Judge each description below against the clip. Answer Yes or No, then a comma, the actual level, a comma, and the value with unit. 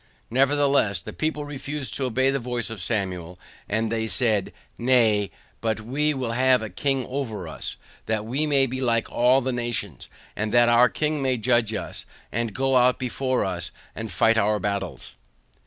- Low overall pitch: Yes, low, 120 Hz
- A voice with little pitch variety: No, average, 3.5 semitones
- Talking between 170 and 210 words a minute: Yes, average, 175 wpm